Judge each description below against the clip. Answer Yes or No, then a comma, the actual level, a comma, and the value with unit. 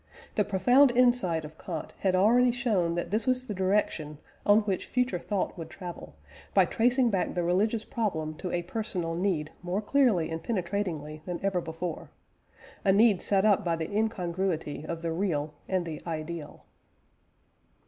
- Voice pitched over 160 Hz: Yes, medium, 185 Hz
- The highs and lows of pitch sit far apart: No, average, 4.3 semitones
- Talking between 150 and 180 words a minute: Yes, average, 165 wpm